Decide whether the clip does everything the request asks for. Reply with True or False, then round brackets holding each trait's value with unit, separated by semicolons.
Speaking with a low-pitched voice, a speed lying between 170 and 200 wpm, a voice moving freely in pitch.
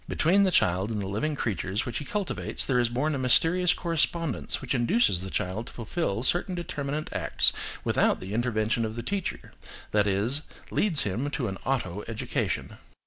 True (125 Hz; 180 wpm; 6.8 semitones)